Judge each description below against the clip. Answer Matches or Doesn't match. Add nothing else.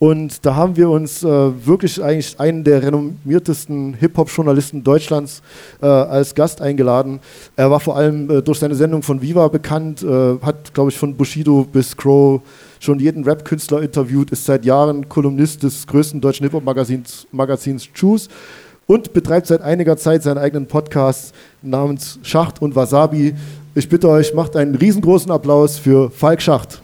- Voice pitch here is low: Doesn't match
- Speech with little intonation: Matches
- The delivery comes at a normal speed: Matches